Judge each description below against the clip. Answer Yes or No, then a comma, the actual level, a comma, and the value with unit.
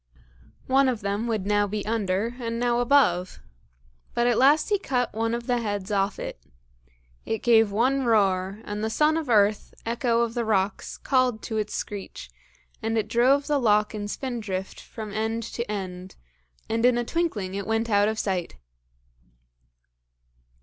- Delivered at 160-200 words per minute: Yes, average, 170 wpm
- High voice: Yes, high, 225 Hz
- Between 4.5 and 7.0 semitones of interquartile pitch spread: No, average, 2.8 semitones